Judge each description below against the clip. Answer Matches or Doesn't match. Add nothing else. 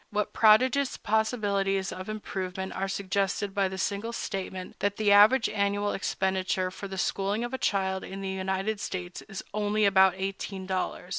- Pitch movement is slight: Matches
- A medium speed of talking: Matches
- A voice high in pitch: Matches